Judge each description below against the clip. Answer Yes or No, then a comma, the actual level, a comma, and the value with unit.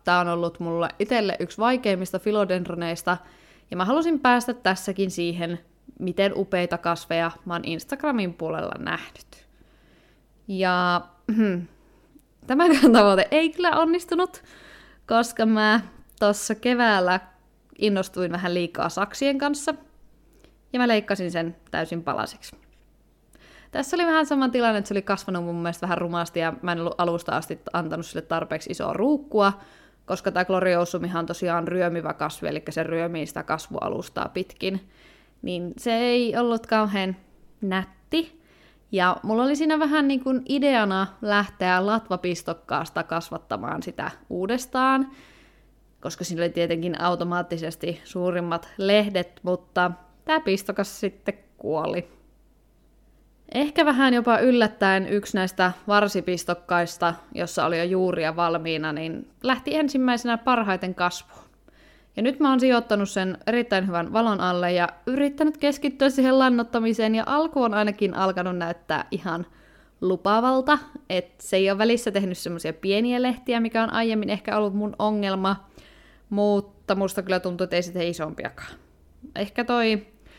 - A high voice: Yes, high, 195 Hz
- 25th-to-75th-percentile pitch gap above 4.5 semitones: Yes, average, 5.0 semitones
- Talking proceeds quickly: No, average, 130 wpm